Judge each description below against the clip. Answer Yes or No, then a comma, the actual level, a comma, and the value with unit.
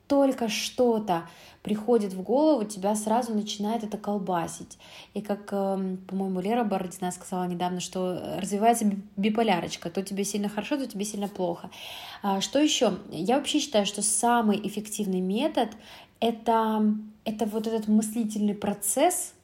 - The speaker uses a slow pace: No, average, 135 wpm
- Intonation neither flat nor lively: Yes, average, 3.0 semitones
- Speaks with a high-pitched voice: Yes, high, 210 Hz